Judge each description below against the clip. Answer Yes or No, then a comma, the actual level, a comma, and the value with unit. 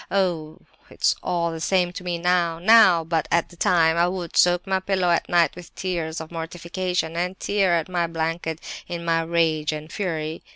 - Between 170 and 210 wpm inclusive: Yes, average, 190 wpm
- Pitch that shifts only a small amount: Yes, narrow, 1.7 semitones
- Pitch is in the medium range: Yes, medium, 170 Hz